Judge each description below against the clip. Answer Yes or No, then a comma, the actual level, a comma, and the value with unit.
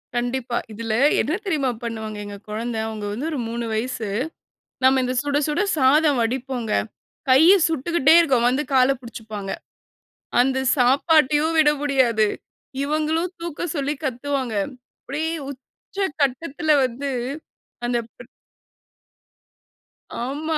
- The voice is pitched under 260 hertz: No, very high, 265 Hz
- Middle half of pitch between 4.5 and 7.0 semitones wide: No, average, 4.0 semitones